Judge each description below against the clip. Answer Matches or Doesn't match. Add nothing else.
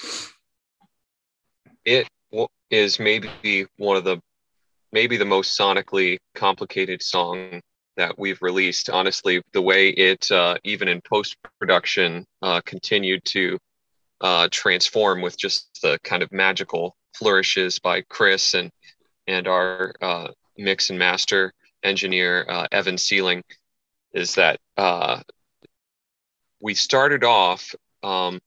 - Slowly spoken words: Matches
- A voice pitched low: Matches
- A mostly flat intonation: Matches